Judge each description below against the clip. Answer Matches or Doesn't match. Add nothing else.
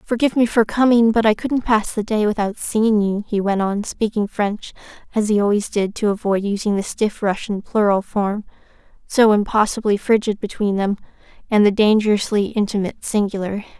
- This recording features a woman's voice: Matches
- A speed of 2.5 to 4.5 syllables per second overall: Doesn't match